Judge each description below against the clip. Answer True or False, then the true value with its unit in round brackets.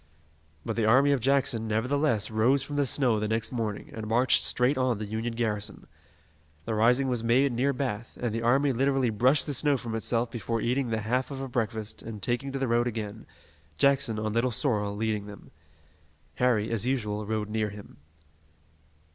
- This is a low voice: True (115 Hz)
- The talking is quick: False (190 wpm)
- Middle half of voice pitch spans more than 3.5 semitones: False (3.1 semitones)